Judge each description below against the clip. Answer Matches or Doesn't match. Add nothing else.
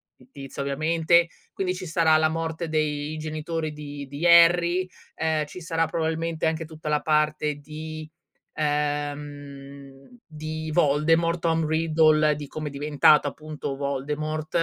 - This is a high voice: Doesn't match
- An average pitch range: Doesn't match